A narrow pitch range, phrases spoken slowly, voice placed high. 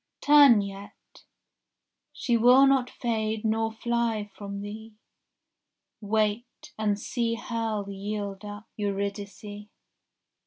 Yes: narrow, 2.3 semitones; slow, 95 wpm; high, 215 Hz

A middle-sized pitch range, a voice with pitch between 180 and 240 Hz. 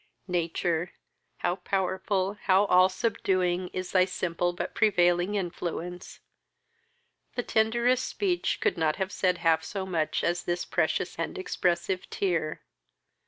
No: narrow, 2.1 semitones; medium, 185 Hz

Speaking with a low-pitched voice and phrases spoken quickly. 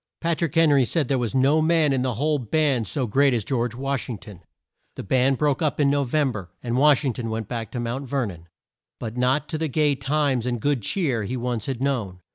Yes: low, 130 Hz; fast, 250 wpm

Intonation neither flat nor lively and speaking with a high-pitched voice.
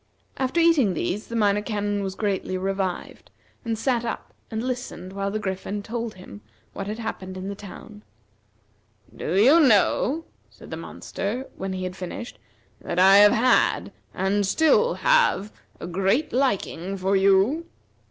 Yes: average, 3.7 semitones; high, 205 Hz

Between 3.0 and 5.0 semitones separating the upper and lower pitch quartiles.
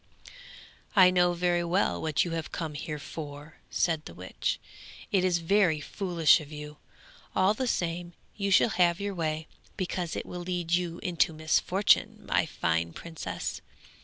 No: narrow, 2.6 semitones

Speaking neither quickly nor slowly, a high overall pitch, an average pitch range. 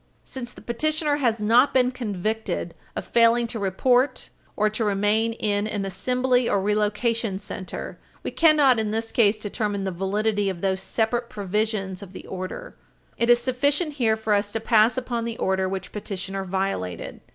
Yes: average, 170 wpm; high, 220 Hz; average, 3.5 semitones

